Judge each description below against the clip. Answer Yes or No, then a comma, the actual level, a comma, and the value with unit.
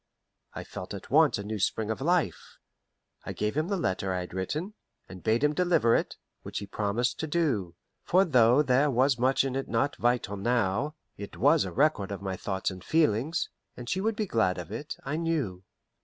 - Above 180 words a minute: Yes, fast, 205 wpm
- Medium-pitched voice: No, low, 120 Hz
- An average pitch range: No, wide, 7.0 semitones